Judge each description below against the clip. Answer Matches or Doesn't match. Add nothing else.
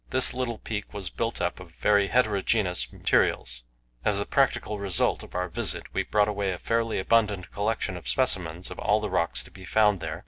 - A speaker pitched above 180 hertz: Doesn't match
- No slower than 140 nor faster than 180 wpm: Doesn't match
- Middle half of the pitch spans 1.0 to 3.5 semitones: Matches